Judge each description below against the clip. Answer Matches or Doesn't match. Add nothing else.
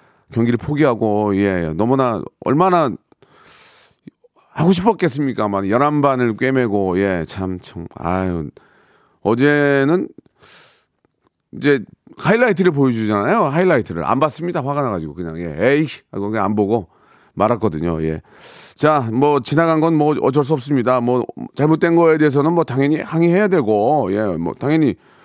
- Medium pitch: Doesn't match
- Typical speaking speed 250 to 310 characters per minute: Matches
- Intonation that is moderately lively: Doesn't match